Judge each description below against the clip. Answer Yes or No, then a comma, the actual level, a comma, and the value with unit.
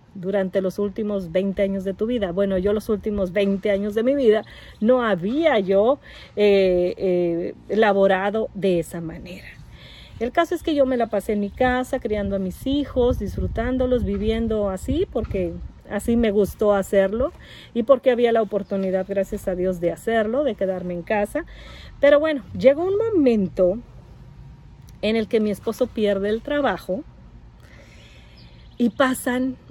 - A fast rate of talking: No, average, 160 wpm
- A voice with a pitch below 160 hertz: No, high, 210 Hz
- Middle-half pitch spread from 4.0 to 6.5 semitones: Yes, average, 4.3 semitones